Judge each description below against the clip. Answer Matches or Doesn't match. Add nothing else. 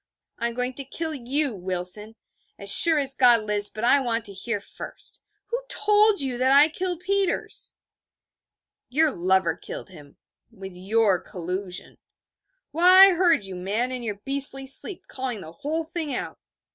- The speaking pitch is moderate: Doesn't match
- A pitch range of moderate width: Doesn't match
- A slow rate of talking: Doesn't match